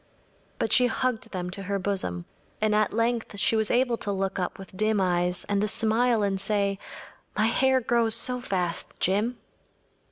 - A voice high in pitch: Yes, high, 210 Hz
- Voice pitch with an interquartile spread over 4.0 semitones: No, average, 3.1 semitones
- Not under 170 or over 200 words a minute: Yes, average, 180 wpm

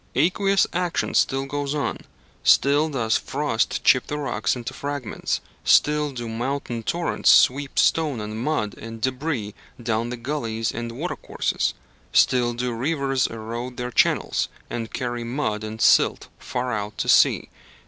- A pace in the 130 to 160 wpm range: Yes, average, 145 wpm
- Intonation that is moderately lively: Yes, average, 4.0 semitones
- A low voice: Yes, low, 125 Hz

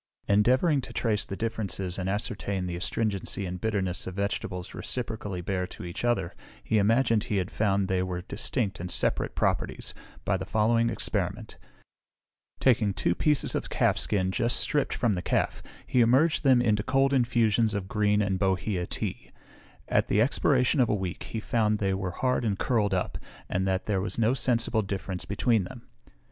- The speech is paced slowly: No, average, 180 wpm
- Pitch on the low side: Yes, low, 105 Hz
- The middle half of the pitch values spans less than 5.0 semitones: Yes, average, 3.7 semitones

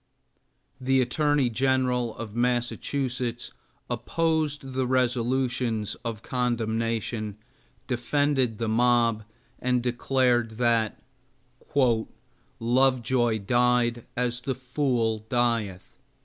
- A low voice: Yes, low, 120 Hz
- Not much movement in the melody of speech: Yes, narrow, 1.9 semitones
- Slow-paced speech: Yes, slow, 80 wpm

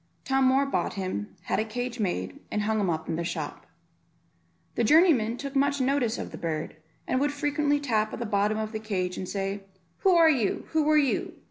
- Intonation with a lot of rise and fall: Yes, wide, 6.0 semitones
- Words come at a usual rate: No, fast, 215 wpm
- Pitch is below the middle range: No, high, 230 Hz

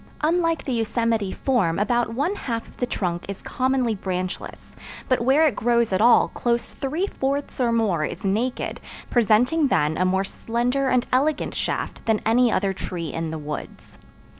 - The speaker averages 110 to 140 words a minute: No, average, 170 wpm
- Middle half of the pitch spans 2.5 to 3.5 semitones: No, average, 5.1 semitones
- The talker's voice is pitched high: Yes, high, 235 Hz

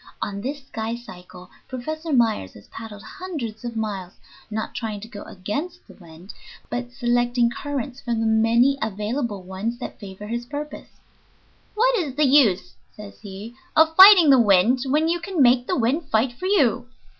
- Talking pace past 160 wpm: Yes, average, 170 wpm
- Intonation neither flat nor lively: Yes, average, 5.0 semitones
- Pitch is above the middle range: Yes, high, 240 Hz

